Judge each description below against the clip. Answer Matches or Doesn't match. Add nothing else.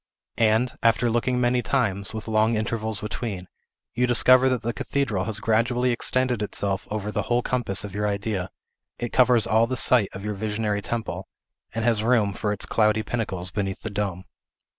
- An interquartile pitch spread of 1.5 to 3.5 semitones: Matches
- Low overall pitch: Matches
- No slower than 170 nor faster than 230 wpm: Matches